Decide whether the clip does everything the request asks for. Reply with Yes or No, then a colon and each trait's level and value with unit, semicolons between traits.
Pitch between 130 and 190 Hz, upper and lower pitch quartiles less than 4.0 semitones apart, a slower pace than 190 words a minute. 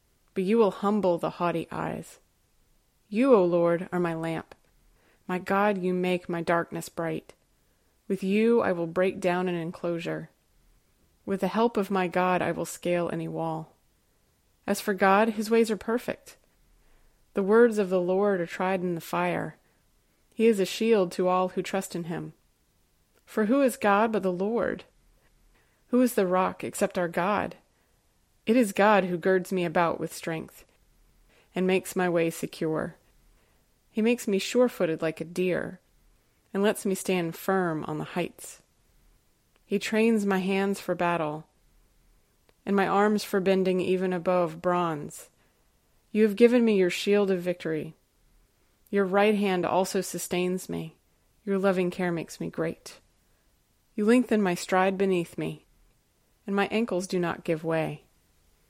Yes: medium, 185 Hz; average, 2.7 semitones; average, 160 wpm